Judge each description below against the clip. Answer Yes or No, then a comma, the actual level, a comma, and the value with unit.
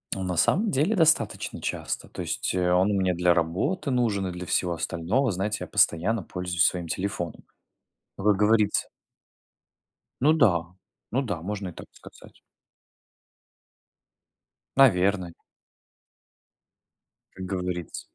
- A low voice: Yes, very low, 95 Hz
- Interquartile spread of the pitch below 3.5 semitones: No, average, 4.1 semitones